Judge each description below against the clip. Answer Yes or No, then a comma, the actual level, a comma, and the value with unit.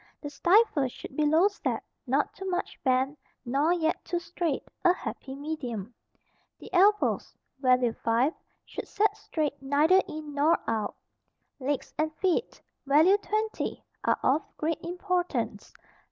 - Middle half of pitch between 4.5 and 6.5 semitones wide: Yes, average, 4.8 semitones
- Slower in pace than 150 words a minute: Yes, average, 140 wpm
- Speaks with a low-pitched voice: No, very high, 310 Hz